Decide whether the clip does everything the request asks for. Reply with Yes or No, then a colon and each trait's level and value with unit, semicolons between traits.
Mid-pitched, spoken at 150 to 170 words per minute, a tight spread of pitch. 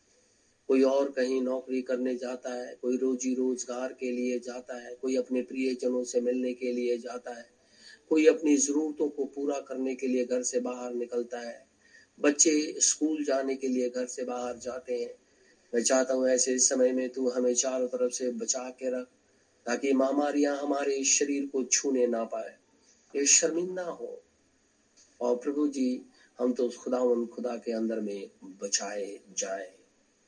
No: low, 130 Hz; average, 165 wpm; narrow, 1.7 semitones